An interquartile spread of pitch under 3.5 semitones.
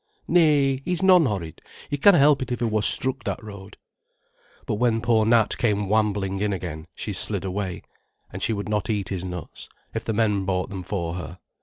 No: average, 4.2 semitones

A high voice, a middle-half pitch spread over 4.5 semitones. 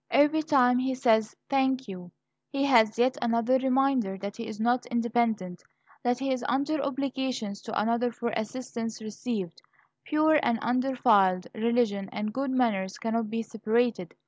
No: high, 235 Hz; average, 3.2 semitones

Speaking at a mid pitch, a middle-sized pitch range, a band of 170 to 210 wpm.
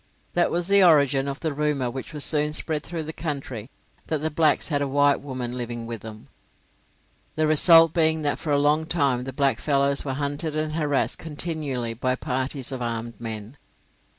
Yes: medium, 145 Hz; average, 3.3 semitones; average, 185 wpm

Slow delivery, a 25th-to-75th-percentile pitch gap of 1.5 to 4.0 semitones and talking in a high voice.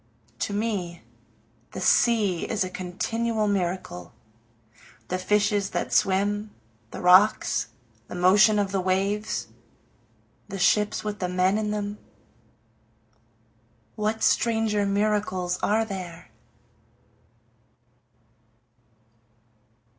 Yes: slow, 95 wpm; narrow, 2.4 semitones; high, 205 Hz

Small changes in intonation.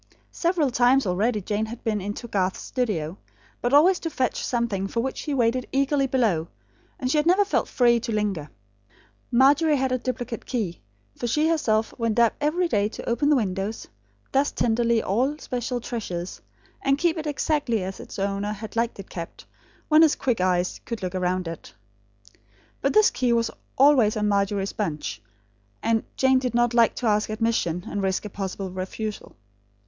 No: average, 4.8 semitones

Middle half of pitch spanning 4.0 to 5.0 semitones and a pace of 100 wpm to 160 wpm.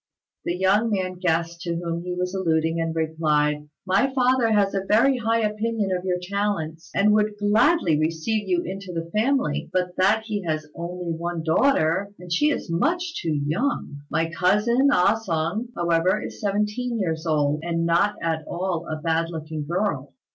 No: average, 4.3 semitones; average, 175 wpm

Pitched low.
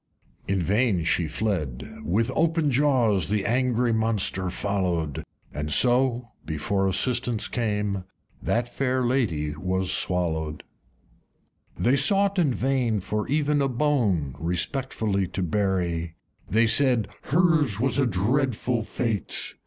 Yes: low, 110 Hz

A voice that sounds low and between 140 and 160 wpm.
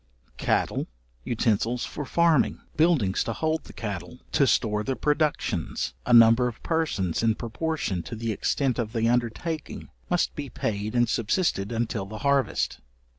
Yes: low, 120 Hz; average, 150 wpm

